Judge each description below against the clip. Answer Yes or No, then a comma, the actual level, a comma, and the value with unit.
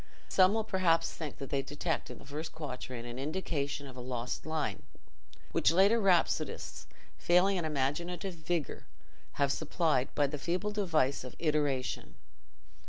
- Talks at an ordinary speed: Yes, average, 150 wpm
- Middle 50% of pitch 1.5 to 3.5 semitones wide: No, average, 4.4 semitones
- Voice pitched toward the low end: No, medium, 155 Hz